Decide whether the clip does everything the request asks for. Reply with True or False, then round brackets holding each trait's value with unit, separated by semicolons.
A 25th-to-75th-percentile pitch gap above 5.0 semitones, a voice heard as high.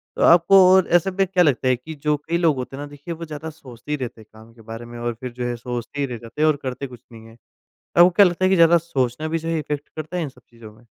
False (5.5 semitones; 145 Hz)